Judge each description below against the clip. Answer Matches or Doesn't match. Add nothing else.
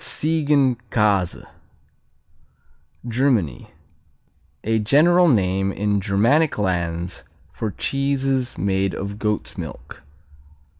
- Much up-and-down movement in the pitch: Matches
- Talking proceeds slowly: Matches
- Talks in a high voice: Doesn't match